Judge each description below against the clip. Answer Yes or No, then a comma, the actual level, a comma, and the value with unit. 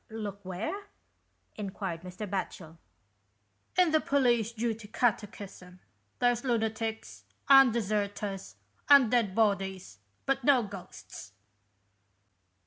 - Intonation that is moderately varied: Yes, average, 3.8 semitones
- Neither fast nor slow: No, slow, 105 wpm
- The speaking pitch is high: Yes, high, 215 Hz